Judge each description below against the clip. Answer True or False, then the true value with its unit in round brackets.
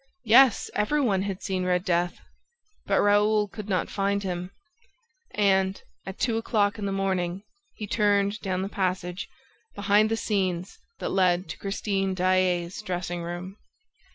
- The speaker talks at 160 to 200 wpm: False (150 wpm)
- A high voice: True (195 Hz)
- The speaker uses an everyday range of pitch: False (2.1 semitones)